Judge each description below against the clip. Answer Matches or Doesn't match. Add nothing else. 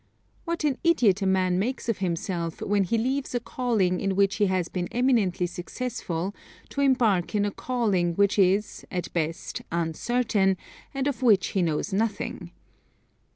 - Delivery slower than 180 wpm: Matches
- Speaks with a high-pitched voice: Matches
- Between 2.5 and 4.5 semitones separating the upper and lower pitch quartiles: Doesn't match